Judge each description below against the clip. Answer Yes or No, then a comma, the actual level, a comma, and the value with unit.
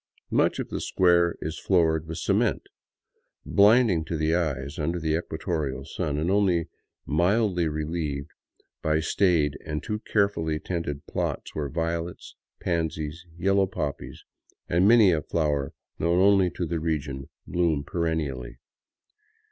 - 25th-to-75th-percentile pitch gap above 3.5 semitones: No, narrow, 2.6 semitones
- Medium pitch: No, very low, 80 Hz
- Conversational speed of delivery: No, slow, 130 wpm